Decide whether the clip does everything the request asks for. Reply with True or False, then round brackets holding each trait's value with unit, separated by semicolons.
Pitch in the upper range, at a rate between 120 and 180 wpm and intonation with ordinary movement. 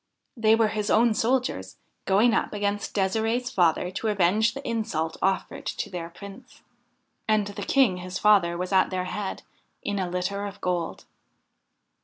True (200 Hz; 160 wpm; 3.3 semitones)